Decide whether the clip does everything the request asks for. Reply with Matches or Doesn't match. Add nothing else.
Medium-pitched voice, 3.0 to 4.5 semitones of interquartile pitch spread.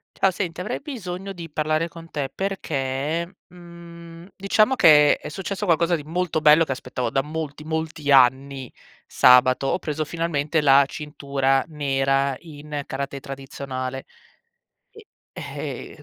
Matches